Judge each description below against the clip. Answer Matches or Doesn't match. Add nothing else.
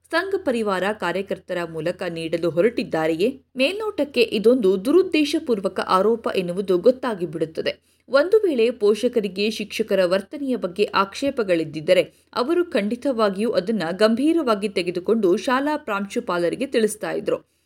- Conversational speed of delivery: Matches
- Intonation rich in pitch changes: Matches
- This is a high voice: Matches